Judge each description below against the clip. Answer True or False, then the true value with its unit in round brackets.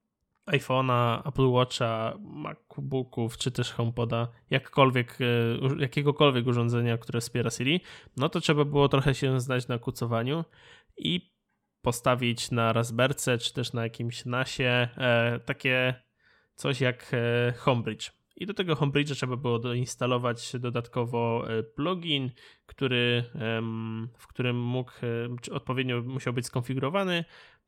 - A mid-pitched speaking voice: False (125 Hz)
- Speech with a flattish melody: True (2.3 semitones)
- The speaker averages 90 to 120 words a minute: True (115 wpm)